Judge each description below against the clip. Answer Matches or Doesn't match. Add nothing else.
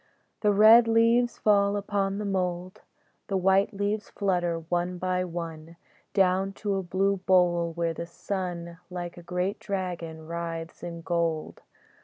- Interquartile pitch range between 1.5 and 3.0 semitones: Matches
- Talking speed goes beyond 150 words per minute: Doesn't match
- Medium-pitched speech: Matches